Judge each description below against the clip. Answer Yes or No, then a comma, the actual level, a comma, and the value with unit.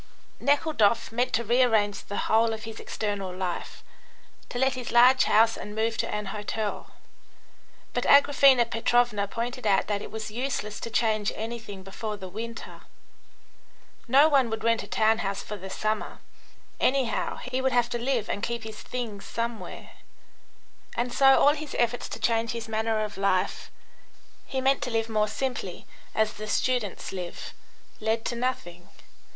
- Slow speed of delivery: No, average, 165 wpm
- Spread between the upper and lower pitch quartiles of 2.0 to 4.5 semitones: Yes, narrow, 2.6 semitones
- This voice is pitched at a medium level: No, high, 225 Hz